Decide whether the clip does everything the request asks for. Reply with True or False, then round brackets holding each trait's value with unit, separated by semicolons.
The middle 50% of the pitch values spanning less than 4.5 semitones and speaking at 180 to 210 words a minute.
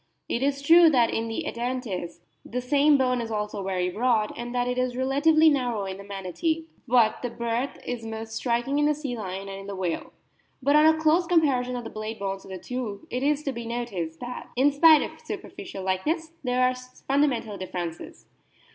False (5.0 semitones; 205 wpm)